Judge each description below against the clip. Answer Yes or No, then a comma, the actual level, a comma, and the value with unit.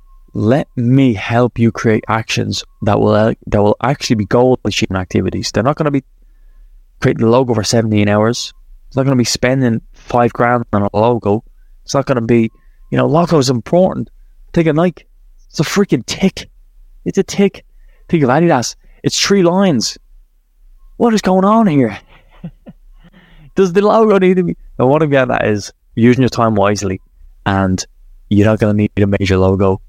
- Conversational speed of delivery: Yes, average, 190 wpm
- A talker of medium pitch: No, low, 120 Hz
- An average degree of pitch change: No, wide, 7.1 semitones